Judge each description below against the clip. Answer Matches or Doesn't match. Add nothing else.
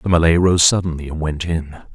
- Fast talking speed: Matches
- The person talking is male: Matches